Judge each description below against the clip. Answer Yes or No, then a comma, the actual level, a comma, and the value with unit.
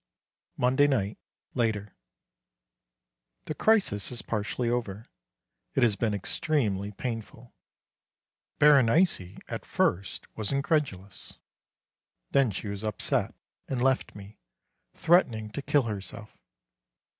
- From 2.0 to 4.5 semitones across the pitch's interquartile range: No, average, 4.9 semitones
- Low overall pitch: Yes, low, 115 Hz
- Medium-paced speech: No, slow, 100 wpm